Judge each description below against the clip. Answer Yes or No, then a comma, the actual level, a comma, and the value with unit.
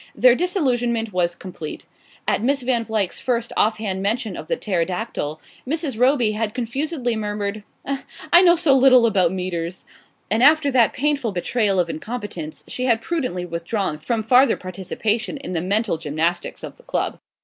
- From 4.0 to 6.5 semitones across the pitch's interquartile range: Yes, wide, 5.5 semitones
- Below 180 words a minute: Yes, average, 165 wpm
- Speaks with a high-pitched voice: Yes, high, 220 Hz